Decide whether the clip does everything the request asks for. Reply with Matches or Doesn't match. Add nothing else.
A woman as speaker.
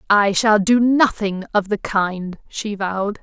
Matches